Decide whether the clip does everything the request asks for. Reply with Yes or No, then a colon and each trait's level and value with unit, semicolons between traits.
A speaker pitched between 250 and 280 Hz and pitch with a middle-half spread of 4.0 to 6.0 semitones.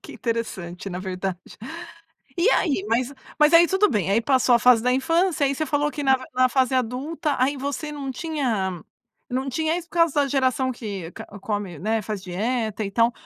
Yes: very high, 255 Hz; wide, 5.4 semitones